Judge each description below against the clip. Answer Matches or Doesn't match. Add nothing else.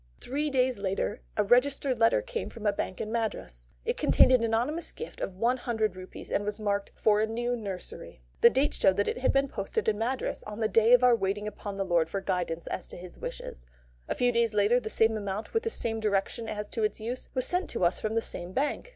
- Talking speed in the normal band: Doesn't match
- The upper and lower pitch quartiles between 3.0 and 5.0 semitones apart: Matches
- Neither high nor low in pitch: Doesn't match